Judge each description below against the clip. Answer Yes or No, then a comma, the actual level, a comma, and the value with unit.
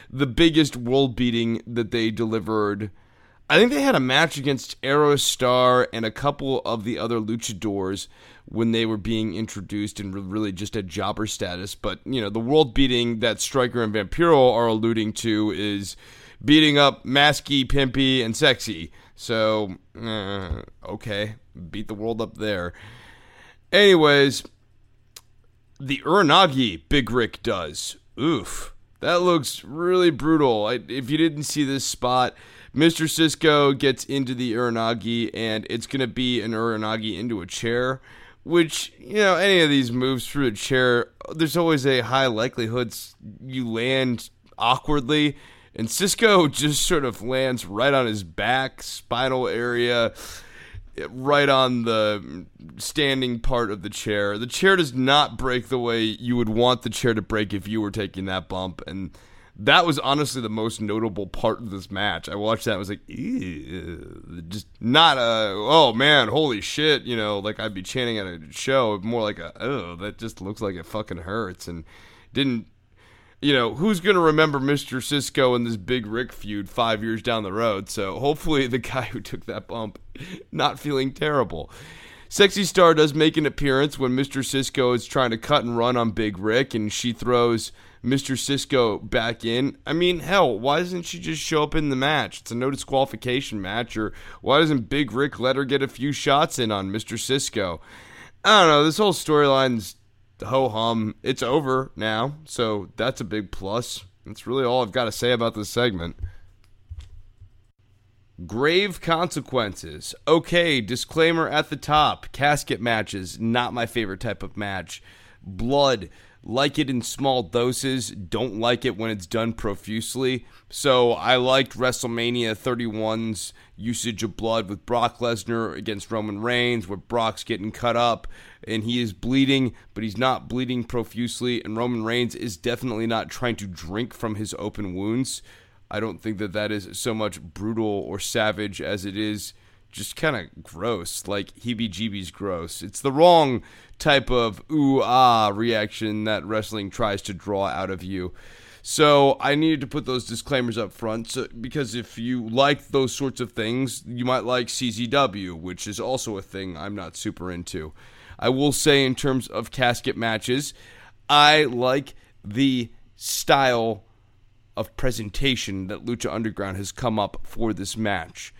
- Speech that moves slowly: No, average, 170 wpm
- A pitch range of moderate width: Yes, average, 4.0 semitones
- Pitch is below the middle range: Yes, low, 115 Hz